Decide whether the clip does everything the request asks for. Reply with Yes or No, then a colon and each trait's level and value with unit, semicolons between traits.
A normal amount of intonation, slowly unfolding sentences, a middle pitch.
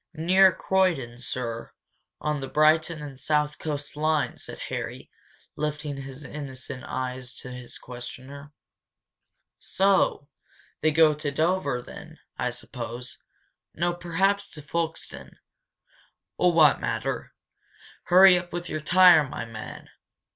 Yes: average, 4.4 semitones; slow, 120 wpm; medium, 150 Hz